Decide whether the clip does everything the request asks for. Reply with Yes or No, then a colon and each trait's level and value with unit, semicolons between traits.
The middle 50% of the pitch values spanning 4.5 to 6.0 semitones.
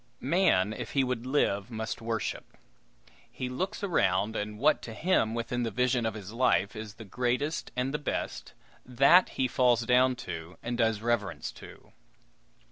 No: average, 2.7 semitones